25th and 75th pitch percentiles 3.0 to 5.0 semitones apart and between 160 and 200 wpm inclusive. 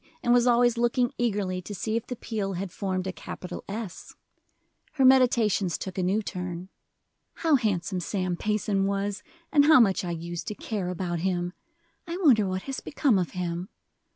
Yes: average, 4.6 semitones; average, 180 wpm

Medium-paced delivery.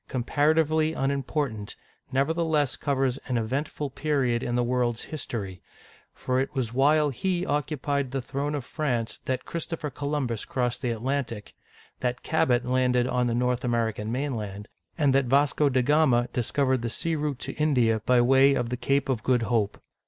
Yes: average, 165 wpm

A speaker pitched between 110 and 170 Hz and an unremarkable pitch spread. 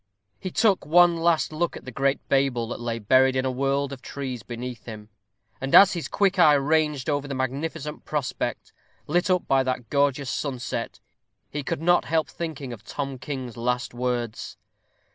Yes: medium, 140 Hz; average, 3.7 semitones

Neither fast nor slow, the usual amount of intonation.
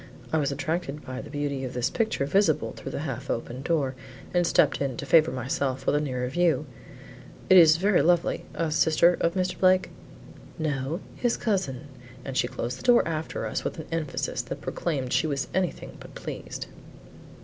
Yes: average, 185 wpm; average, 4.3 semitones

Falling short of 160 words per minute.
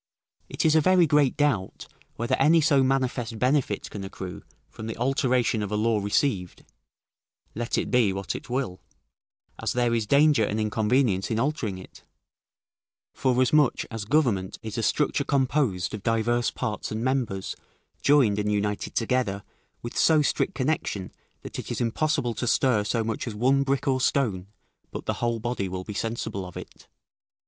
No: average, 170 wpm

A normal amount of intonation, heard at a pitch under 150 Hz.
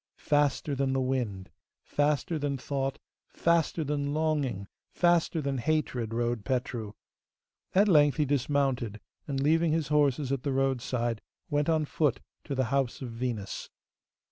Yes: average, 3.1 semitones; medium, 140 Hz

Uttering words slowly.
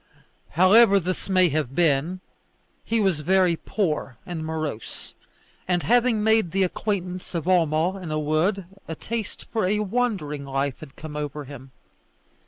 No: average, 150 wpm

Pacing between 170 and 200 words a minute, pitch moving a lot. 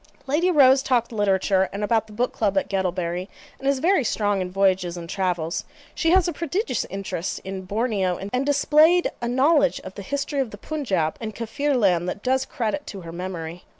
Yes: average, 190 wpm; wide, 6.5 semitones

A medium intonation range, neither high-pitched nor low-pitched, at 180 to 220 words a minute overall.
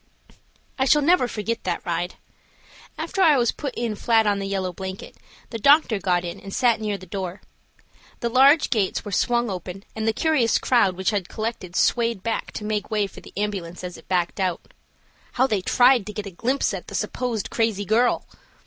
No: average, 4.1 semitones; high, 215 Hz; average, 200 wpm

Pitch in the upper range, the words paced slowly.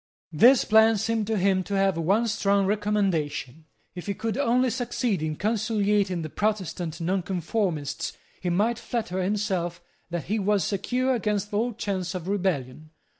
No: high, 200 Hz; average, 150 wpm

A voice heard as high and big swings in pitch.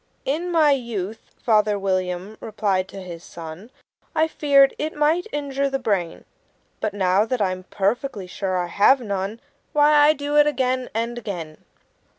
Yes: high, 220 Hz; wide, 6.7 semitones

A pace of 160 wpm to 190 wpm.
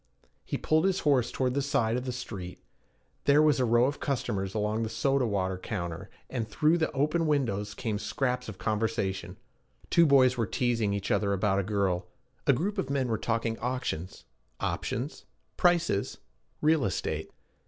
Yes: average, 170 wpm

